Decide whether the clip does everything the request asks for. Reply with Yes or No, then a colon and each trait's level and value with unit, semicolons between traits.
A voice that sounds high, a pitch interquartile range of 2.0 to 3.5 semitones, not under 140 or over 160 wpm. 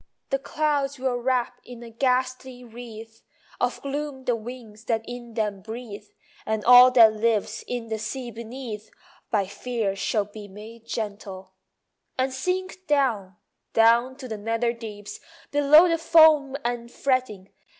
Yes: high, 235 Hz; average, 3.2 semitones; average, 145 wpm